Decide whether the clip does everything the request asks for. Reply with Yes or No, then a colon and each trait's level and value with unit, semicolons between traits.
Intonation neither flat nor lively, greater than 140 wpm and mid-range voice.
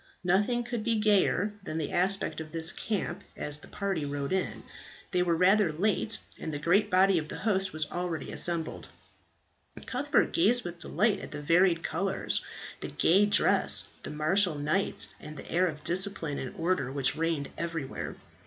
Yes: average, 4.2 semitones; average, 175 wpm; medium, 180 Hz